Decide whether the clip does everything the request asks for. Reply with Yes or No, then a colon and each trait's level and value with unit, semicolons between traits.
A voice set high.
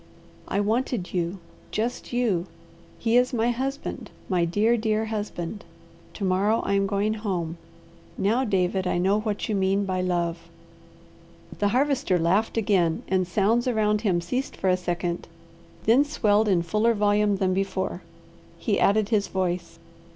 Yes: high, 200 Hz